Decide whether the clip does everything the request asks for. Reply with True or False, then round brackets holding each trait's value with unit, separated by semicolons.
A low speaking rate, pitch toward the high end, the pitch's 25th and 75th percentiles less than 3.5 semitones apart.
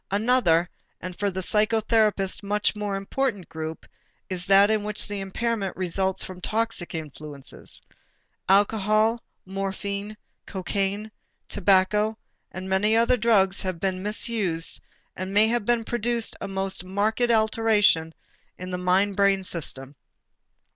True (125 wpm; 200 Hz; 2.6 semitones)